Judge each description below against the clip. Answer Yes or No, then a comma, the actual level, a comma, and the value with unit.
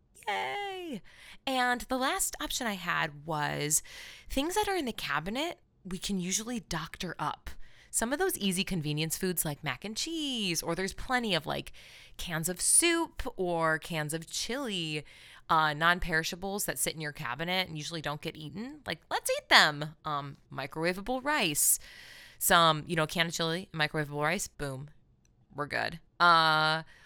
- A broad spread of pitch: Yes, wide, 6.2 semitones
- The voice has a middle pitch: Yes, medium, 170 Hz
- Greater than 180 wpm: No, average, 160 wpm